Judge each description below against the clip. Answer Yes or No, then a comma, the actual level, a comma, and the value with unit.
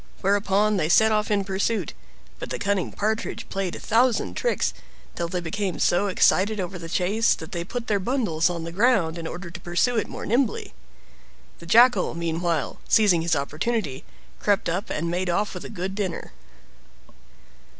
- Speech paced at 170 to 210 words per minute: Yes, average, 175 wpm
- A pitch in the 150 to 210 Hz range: Yes, high, 190 Hz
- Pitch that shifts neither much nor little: Yes, average, 3.8 semitones